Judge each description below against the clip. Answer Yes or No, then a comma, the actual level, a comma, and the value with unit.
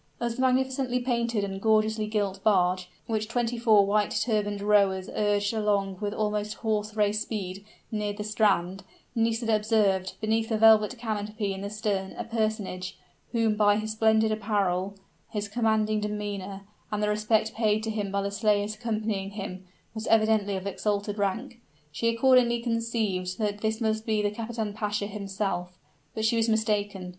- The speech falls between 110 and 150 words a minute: No, average, 165 wpm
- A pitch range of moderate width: No, narrow, 1.6 semitones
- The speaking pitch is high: Yes, high, 210 Hz